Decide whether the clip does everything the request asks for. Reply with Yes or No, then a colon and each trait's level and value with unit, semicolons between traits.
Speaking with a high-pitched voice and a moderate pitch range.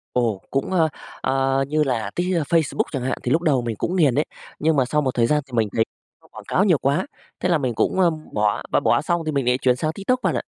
No: medium, 140 Hz; average, 4.9 semitones